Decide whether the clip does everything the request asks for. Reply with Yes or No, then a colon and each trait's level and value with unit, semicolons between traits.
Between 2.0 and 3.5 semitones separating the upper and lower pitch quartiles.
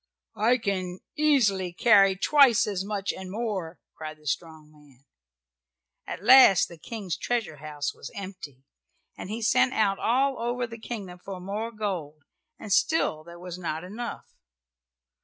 No: average, 5.0 semitones